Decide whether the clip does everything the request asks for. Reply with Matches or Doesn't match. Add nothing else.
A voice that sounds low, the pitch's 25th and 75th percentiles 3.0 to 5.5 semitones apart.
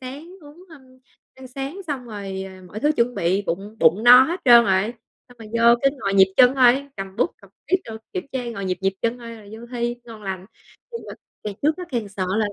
Doesn't match